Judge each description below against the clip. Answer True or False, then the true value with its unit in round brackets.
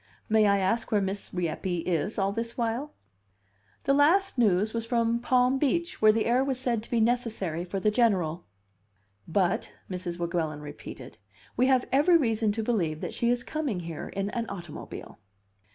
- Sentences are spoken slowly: False (175 wpm)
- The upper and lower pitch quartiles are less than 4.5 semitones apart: False (4.9 semitones)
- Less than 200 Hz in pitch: False (220 Hz)